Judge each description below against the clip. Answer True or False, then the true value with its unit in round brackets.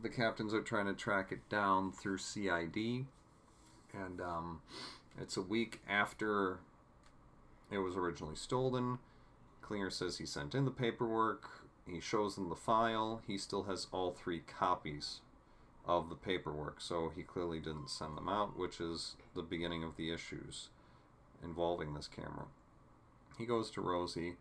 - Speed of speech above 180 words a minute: False (150 wpm)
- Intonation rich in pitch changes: False (4.7 semitones)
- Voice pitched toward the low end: True (95 Hz)